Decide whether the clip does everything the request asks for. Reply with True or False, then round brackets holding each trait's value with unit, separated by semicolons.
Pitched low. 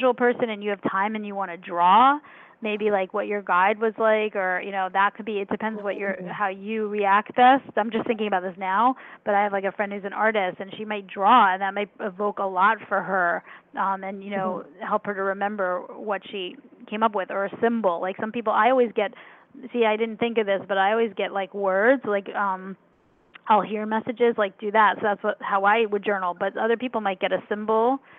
False (205 Hz)